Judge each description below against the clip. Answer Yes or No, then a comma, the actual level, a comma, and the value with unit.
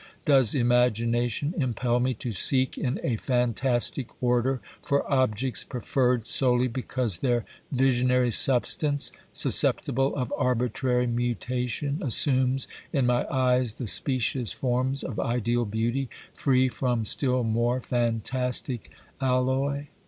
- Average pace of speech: No, slow, 115 wpm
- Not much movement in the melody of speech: Yes, narrow, 1.6 semitones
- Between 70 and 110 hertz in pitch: No, low, 125 Hz